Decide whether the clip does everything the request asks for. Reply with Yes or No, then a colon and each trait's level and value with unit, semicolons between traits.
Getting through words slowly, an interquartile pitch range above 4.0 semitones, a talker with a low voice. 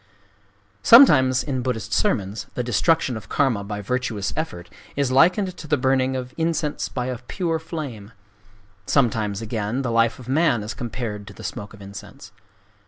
No: average, 160 wpm; average, 5.1 semitones; low, 125 Hz